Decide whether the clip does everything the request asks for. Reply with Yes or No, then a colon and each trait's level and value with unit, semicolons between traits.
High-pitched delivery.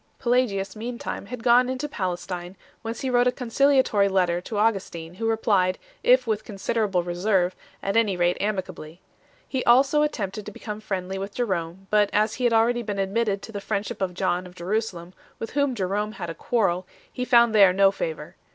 Yes: high, 205 Hz